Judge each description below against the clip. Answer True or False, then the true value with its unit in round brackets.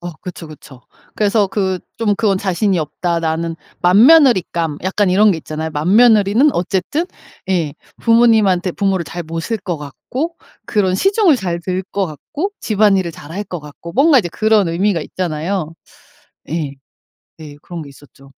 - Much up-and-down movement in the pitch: False (4.4 semitones)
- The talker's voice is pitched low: False (185 Hz)